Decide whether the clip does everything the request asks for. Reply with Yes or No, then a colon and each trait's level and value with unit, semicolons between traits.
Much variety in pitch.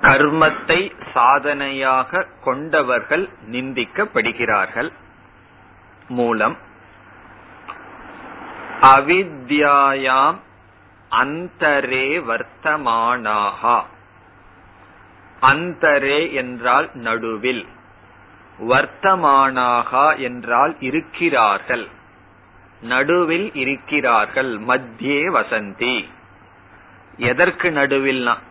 No: average, 4.5 semitones